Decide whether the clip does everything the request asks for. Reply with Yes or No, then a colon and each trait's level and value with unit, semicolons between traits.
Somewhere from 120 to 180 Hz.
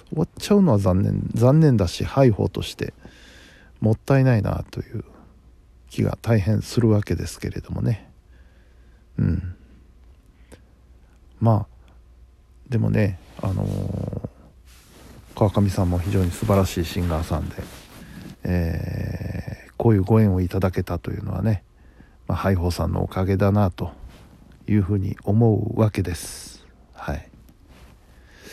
No: very low, 95 Hz